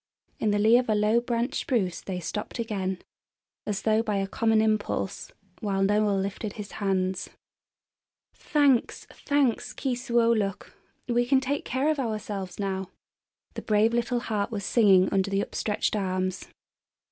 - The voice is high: Yes, high, 215 Hz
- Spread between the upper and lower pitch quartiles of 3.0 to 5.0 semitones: Yes, average, 3.3 semitones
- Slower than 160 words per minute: Yes, average, 145 wpm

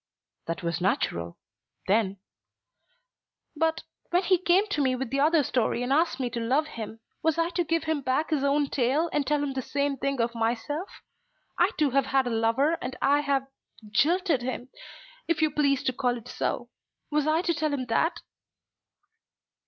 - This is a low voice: No, very high, 275 Hz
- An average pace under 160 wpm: No, average, 185 wpm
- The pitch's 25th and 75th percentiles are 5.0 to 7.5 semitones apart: No, average, 4.2 semitones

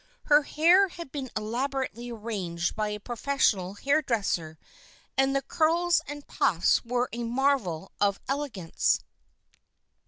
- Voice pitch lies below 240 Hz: No, high, 245 Hz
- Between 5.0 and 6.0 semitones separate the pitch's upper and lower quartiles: Yes, wide, 5.5 semitones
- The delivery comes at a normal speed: No, slow, 125 wpm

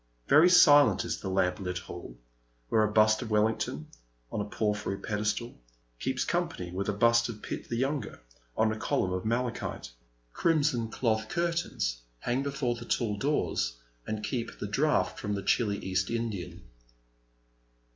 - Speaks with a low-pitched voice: Yes, low, 110 Hz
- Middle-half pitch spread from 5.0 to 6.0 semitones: No, average, 4.3 semitones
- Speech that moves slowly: No, average, 155 wpm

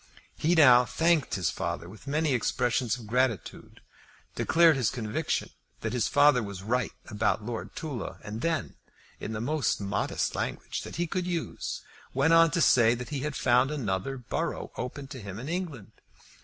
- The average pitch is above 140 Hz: No, low, 125 Hz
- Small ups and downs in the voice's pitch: No, wide, 5.5 semitones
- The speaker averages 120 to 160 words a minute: No, average, 170 wpm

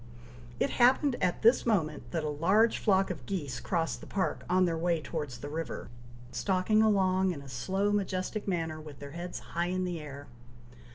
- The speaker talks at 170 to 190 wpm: Yes, average, 185 wpm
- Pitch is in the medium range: Yes, medium, 175 Hz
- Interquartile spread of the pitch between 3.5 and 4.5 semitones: Yes, average, 4.2 semitones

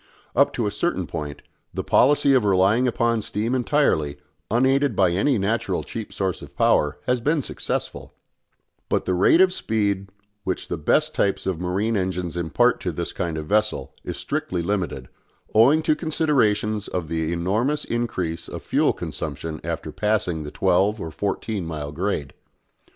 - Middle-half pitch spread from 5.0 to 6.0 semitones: Yes, wide, 5.5 semitones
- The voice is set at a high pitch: No, low, 100 Hz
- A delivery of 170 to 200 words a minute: No, average, 160 wpm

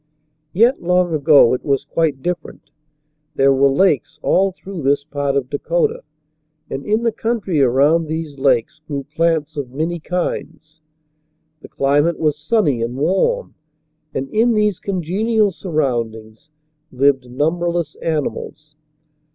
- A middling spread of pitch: Yes, average, 4.5 semitones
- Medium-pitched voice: Yes, medium, 155 Hz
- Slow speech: Yes, slow, 130 wpm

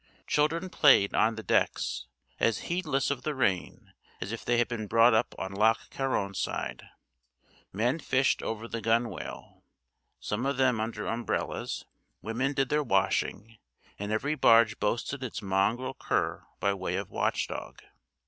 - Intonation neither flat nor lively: Yes, average, 4.2 semitones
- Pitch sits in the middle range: No, low, 115 Hz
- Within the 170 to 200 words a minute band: No, average, 155 wpm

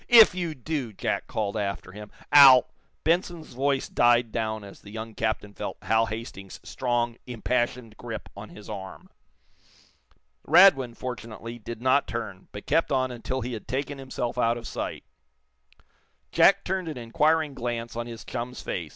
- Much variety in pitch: No, average, 3.4 semitones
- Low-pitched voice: Yes, low, 120 Hz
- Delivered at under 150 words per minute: No, average, 160 wpm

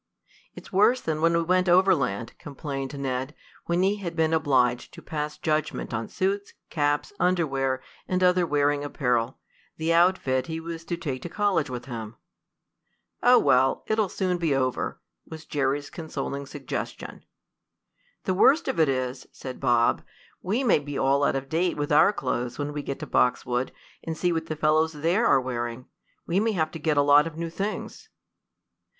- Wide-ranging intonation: No, average, 4.2 semitones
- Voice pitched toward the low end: No, medium, 150 Hz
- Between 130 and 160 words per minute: No, average, 175 wpm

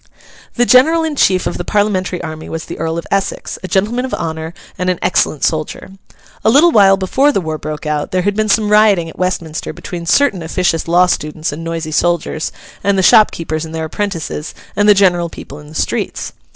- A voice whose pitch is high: No, medium, 180 Hz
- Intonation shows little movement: No, average, 4.2 semitones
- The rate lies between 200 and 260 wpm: Yes, fast, 205 wpm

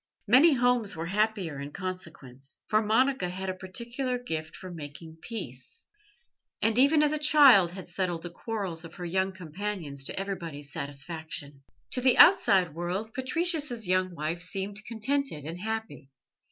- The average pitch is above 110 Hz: Yes, high, 190 Hz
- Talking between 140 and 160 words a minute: Yes, average, 155 wpm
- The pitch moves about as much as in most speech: No, wide, 5.8 semitones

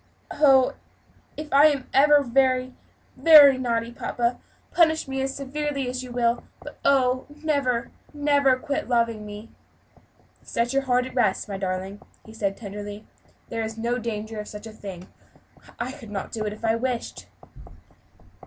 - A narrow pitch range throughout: No, average, 3.7 semitones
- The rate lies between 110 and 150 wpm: No, average, 160 wpm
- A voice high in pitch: Yes, high, 245 Hz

